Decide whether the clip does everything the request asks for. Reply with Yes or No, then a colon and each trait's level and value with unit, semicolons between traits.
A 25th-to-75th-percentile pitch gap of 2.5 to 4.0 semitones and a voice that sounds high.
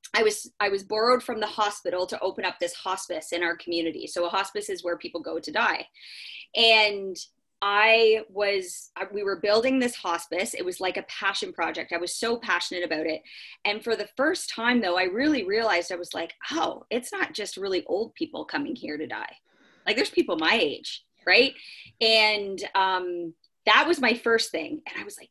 No: average, 4.4 semitones; high, 205 Hz